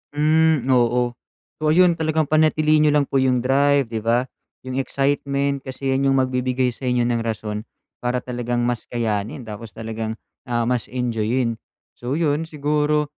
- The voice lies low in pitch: Yes, low, 130 Hz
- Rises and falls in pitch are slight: No, average, 3.5 semitones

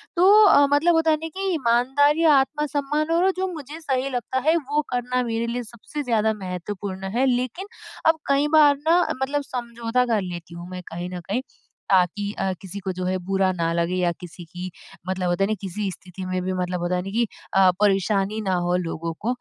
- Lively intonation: Yes, wide, 7.5 semitones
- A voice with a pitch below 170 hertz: No, high, 225 Hz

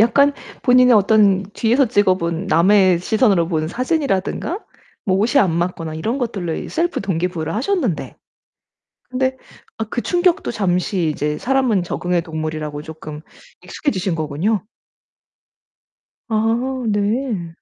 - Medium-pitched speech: No, high, 195 Hz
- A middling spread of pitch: No, wide, 6.4 semitones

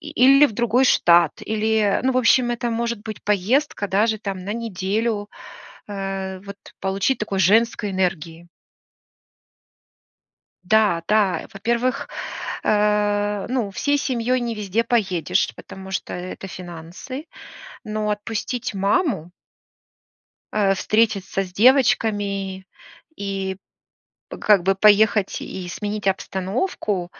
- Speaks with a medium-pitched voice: No, high, 205 Hz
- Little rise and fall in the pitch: No, average, 3.2 semitones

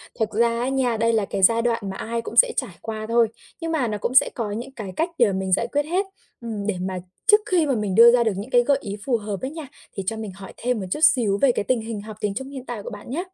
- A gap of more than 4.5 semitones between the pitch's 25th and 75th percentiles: No, average, 3.9 semitones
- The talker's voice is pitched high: Yes, high, 230 Hz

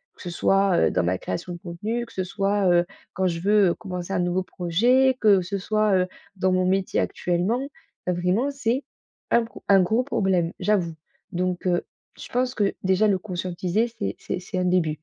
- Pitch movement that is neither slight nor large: Yes, average, 3.2 semitones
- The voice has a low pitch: No, medium, 185 Hz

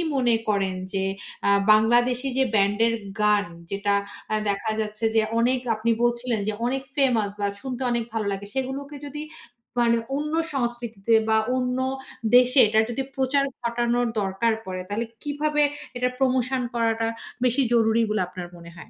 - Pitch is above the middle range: Yes, high, 235 Hz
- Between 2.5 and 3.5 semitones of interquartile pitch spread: Yes, average, 3.1 semitones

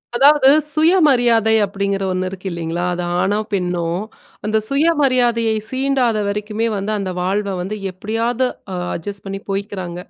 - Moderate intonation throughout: Yes, average, 4.3 semitones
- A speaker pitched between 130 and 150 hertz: No, high, 210 Hz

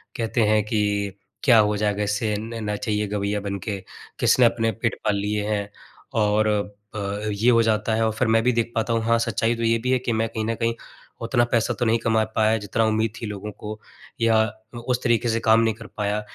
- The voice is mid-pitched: No, low, 110 Hz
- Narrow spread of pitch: Yes, narrow, 1.6 semitones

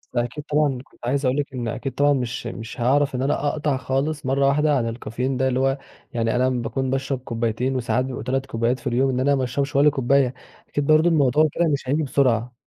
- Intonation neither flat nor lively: No, narrow, 2.3 semitones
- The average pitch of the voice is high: No, low, 135 Hz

